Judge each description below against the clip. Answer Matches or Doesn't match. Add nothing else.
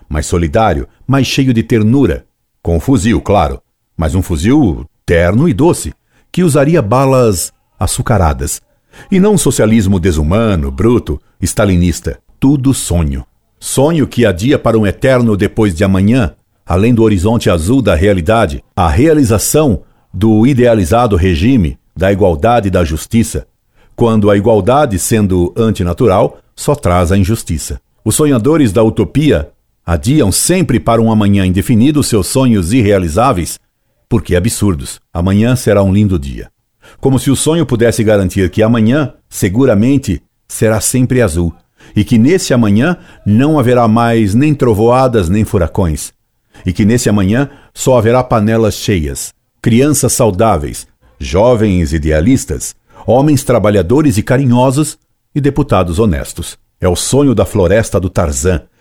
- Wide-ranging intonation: Doesn't match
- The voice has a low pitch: Matches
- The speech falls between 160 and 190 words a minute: Doesn't match